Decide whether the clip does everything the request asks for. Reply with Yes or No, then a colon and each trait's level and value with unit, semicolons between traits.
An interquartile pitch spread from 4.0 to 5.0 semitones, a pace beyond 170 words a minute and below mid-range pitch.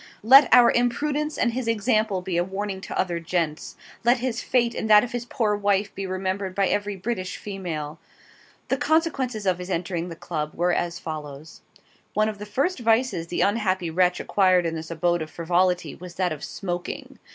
No: average, 4.7 semitones; average, 190 wpm; high, 190 Hz